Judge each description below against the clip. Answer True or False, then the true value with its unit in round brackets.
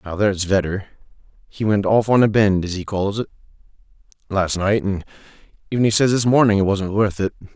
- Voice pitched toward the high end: False (100 Hz)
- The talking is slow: False (200 wpm)